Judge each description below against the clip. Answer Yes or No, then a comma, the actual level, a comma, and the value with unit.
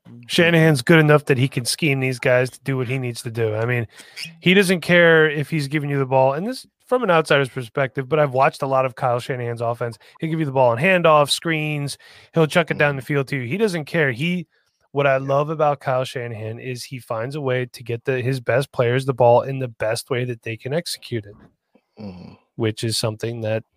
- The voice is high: No, low, 135 Hz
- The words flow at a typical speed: No, fast, 235 wpm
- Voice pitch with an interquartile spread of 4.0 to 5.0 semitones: Yes, average, 4.4 semitones